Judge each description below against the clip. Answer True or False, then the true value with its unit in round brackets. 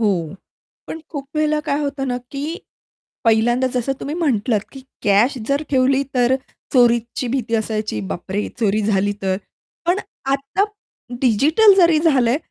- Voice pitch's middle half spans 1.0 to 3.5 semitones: False (4.6 semitones)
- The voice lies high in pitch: True (255 Hz)